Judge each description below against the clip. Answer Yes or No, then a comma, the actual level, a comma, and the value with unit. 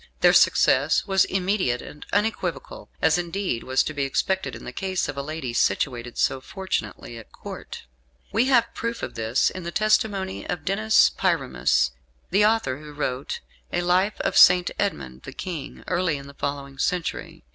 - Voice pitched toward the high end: No, medium, 170 Hz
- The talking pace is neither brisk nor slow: Yes, average, 170 wpm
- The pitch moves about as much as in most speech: No, wide, 6.1 semitones